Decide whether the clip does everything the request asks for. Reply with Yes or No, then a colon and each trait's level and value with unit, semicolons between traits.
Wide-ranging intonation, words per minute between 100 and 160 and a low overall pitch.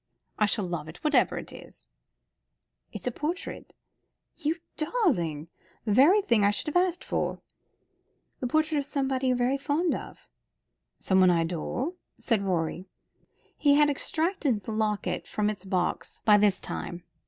No: wide, 8.0 semitones; average, 150 wpm; high, 240 Hz